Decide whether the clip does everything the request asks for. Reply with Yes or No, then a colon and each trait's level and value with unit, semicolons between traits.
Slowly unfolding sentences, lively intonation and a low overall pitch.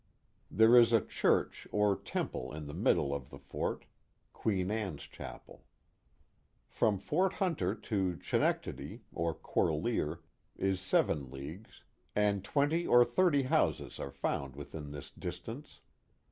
Yes: slow, 130 wpm; wide, 7.3 semitones; very low, 95 Hz